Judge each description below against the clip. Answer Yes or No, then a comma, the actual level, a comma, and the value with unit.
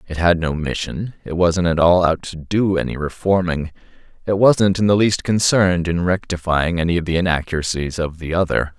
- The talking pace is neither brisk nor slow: Yes, average, 190 wpm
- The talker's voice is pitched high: No, very low, 85 Hz